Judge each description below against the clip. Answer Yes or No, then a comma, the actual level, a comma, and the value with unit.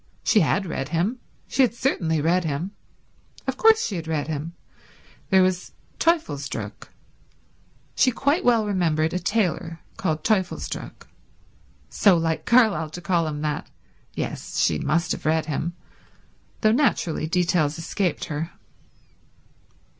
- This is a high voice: No, medium, 170 Hz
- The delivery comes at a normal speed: No, slow, 130 wpm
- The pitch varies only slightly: No, average, 4.8 semitones